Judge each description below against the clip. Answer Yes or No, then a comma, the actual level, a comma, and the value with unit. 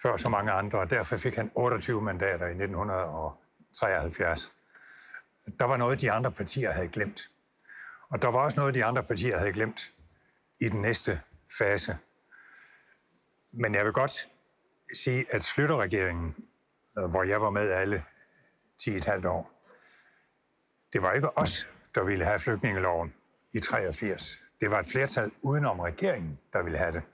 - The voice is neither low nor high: No, low, 105 Hz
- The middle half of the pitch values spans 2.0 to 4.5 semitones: No, average, 5.2 semitones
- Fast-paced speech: No, average, 150 wpm